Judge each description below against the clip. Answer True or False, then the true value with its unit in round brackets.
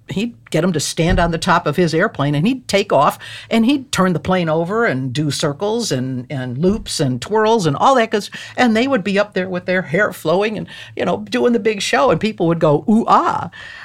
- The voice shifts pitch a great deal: True (5.7 semitones)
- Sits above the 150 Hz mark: True (190 Hz)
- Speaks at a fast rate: True (245 wpm)